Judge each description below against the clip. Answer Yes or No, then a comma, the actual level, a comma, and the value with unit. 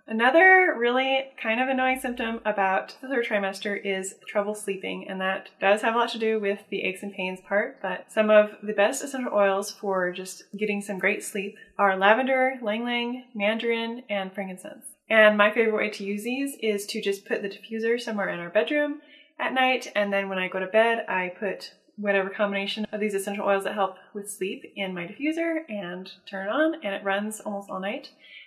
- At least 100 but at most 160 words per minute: No, fast, 205 wpm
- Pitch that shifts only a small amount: No, average, 3.2 semitones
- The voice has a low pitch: No, high, 210 Hz